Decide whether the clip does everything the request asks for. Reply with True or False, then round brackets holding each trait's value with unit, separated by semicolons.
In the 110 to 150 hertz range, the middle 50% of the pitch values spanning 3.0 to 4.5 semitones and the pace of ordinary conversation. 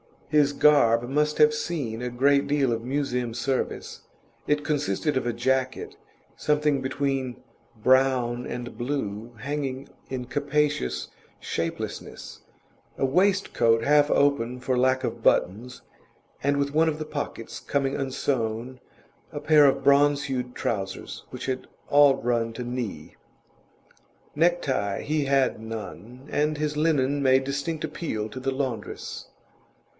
False (135 Hz; 3.3 semitones; 130 wpm)